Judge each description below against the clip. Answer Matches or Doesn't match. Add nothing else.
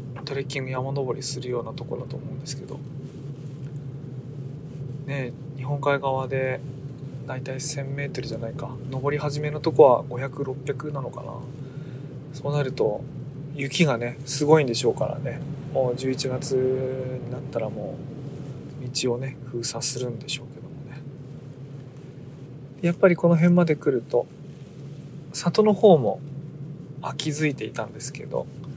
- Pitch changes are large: Doesn't match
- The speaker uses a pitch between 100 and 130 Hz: Doesn't match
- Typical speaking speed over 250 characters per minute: Matches